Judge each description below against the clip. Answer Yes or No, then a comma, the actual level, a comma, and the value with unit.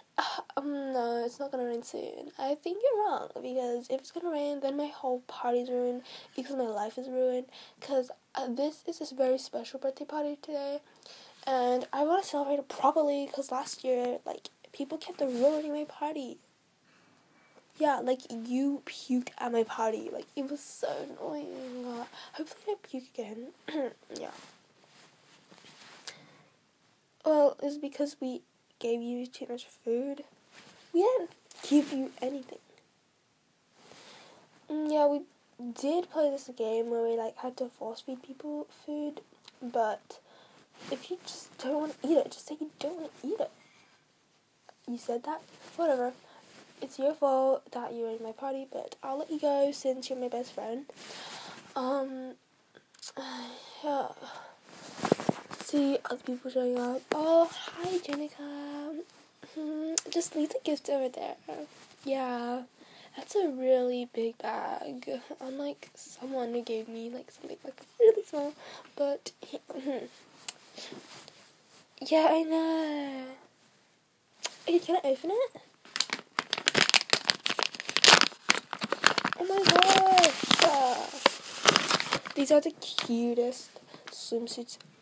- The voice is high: Yes, very high, 275 Hz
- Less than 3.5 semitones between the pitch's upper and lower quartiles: Yes, average, 3.1 semitones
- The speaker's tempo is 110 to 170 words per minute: Yes, slow, 135 wpm